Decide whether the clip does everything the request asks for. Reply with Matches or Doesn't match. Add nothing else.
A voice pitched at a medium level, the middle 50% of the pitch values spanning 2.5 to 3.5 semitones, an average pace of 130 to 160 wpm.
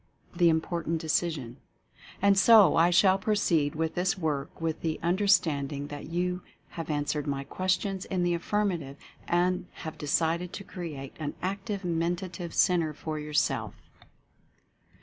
Matches